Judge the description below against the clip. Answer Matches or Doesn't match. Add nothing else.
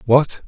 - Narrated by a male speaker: Matches